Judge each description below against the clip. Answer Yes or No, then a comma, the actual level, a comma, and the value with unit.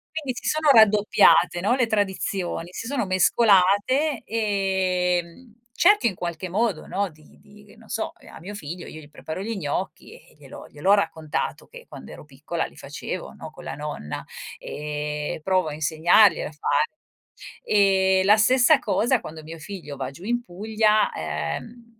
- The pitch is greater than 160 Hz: Yes, high, 190 Hz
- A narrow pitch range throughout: No, wide, 5.4 semitones